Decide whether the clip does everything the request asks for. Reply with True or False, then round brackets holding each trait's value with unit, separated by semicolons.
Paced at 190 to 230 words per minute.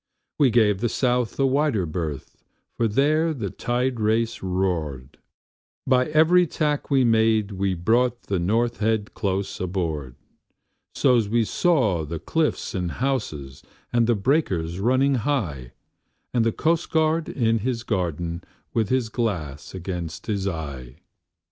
False (135 wpm)